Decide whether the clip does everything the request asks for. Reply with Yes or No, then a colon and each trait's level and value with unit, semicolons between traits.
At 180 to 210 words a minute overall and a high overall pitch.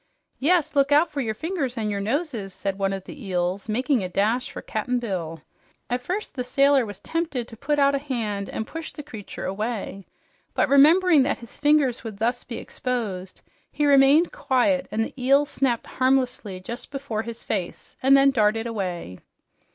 Yes: average, 185 wpm; high, 245 Hz